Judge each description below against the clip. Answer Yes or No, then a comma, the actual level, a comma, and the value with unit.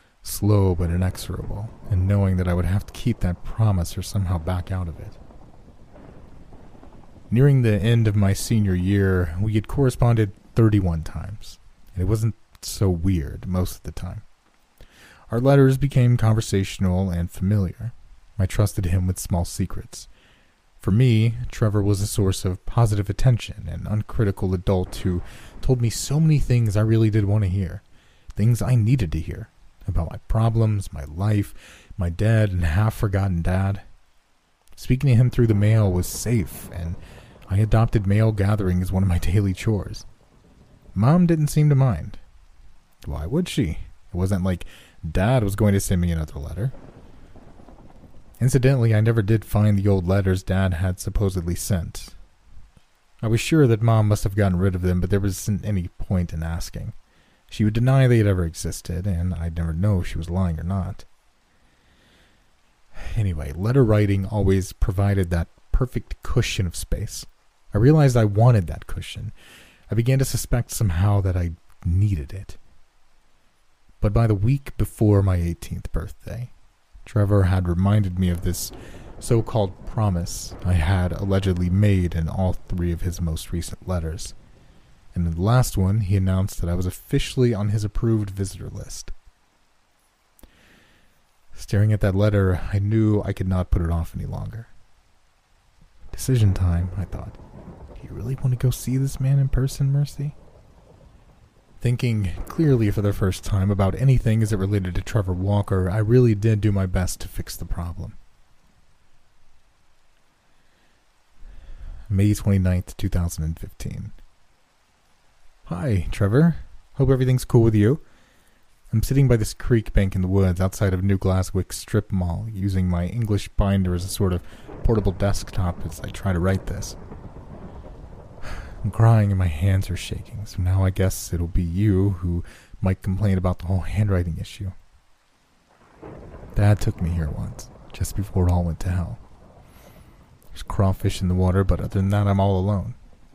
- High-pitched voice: No, very low, 95 Hz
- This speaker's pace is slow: No, average, 165 wpm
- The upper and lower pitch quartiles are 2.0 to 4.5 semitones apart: Yes, average, 3.4 semitones